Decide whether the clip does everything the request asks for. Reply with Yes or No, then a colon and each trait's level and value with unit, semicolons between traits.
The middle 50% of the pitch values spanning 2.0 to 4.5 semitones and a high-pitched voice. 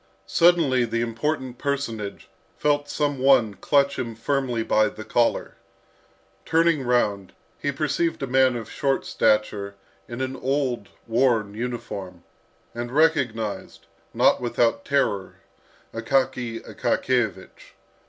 No: average, 3.6 semitones; low, 125 Hz